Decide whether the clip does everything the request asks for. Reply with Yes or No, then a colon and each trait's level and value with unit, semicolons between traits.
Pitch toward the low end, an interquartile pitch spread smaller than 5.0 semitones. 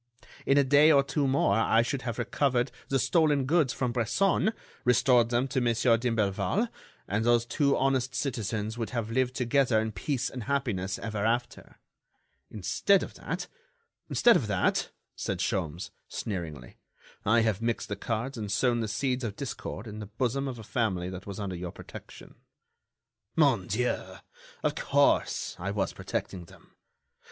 Yes: low, 120 Hz; average, 4.2 semitones